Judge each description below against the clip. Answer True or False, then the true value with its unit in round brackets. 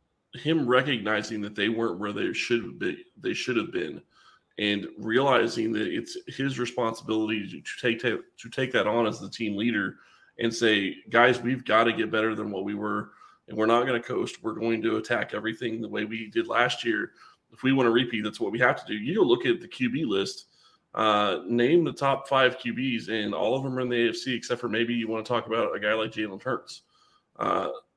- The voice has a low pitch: True (115 Hz)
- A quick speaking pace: True (225 wpm)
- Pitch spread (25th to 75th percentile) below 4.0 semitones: True (2.9 semitones)